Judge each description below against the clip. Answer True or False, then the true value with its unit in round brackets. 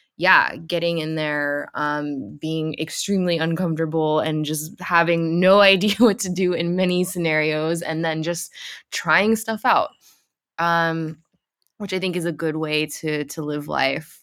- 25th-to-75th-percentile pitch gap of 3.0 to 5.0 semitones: False (2.6 semitones)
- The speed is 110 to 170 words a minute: True (155 wpm)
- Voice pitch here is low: False (165 Hz)